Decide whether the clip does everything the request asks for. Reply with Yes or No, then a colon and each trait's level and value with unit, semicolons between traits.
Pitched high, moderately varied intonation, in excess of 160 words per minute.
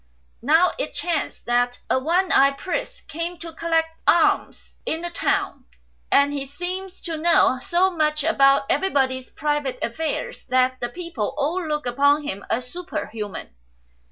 No: very high, 300 Hz; average, 4.8 semitones; average, 150 wpm